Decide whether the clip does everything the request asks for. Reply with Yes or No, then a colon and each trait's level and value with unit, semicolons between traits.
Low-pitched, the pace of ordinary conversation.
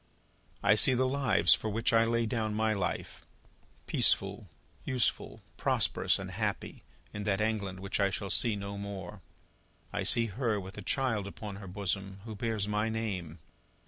Yes: low, 105 Hz; average, 165 wpm